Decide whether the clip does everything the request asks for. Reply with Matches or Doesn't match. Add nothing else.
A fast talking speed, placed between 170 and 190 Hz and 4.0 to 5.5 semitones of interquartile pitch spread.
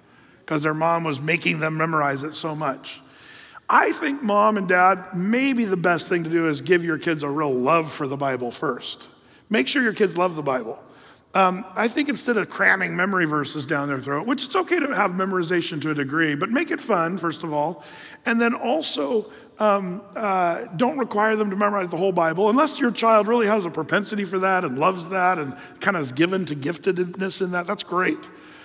Matches